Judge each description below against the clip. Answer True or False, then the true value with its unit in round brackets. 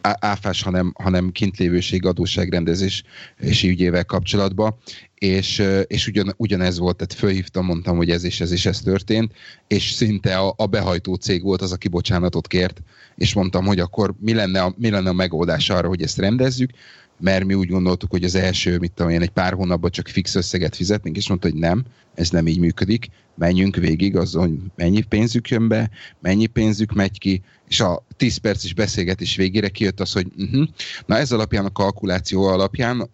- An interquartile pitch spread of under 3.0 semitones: True (2.6 semitones)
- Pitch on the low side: True (95 Hz)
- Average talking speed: False (180 wpm)